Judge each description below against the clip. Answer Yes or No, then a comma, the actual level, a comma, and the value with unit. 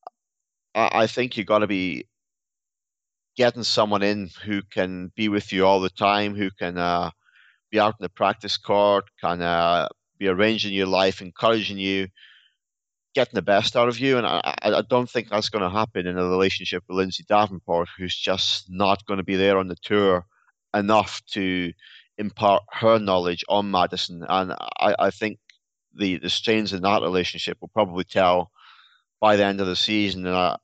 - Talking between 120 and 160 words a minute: No, average, 180 wpm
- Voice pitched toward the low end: Yes, low, 100 Hz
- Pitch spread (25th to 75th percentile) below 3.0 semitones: Yes, narrow, 2.4 semitones